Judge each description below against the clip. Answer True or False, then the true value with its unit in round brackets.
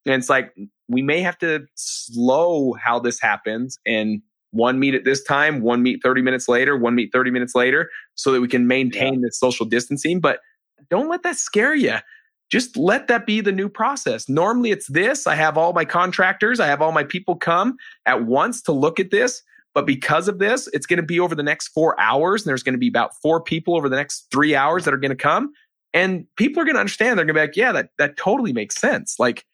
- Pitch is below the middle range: False (155 Hz)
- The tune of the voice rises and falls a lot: True (8.0 semitones)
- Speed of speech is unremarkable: False (240 wpm)